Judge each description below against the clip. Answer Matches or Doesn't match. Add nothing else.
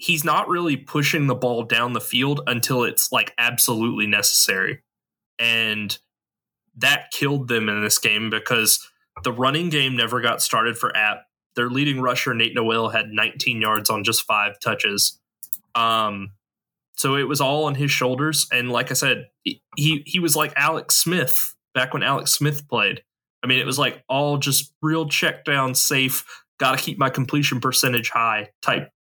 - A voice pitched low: Matches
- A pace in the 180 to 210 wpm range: Doesn't match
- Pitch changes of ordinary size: Matches